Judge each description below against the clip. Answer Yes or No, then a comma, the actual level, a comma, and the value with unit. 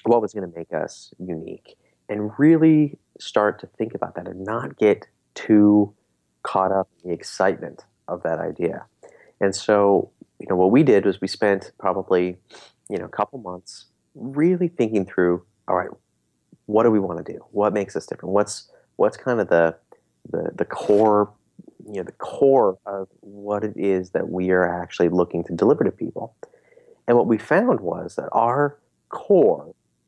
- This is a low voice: Yes, low, 100 Hz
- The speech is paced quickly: No, average, 180 wpm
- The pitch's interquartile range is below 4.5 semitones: Yes, average, 3.3 semitones